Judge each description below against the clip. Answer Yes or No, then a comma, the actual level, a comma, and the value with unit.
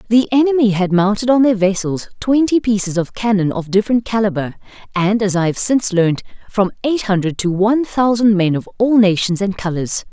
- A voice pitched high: Yes, high, 205 Hz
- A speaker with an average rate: Yes, average, 190 wpm